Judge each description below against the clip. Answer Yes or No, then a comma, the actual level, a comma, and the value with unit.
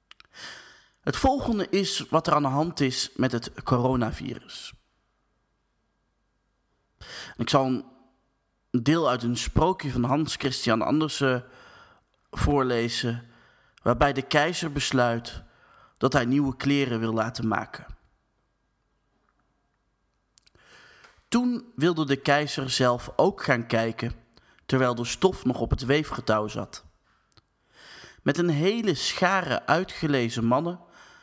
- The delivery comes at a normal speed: No, slow, 110 wpm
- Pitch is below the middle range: Yes, low, 130 Hz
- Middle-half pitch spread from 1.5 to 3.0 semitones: No, average, 4.0 semitones